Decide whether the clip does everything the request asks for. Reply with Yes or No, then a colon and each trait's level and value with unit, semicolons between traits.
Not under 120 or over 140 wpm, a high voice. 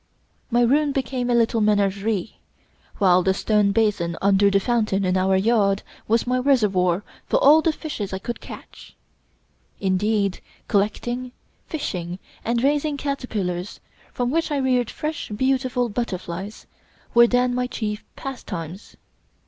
Yes: slow, 135 wpm; high, 220 Hz